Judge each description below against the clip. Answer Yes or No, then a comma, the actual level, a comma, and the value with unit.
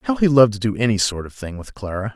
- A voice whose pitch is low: Yes, low, 110 Hz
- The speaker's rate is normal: No, fast, 305 wpm